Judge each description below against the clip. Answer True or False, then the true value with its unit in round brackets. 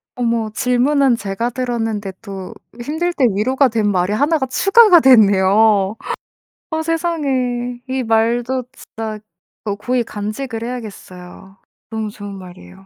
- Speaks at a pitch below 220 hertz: False (230 Hz)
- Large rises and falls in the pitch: False (4.2 semitones)